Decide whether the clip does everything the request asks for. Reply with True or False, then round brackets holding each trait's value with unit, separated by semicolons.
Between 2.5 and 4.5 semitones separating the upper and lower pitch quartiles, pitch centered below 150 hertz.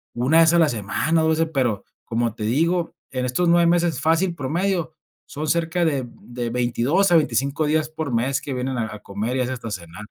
False (5.3 semitones; 140 Hz)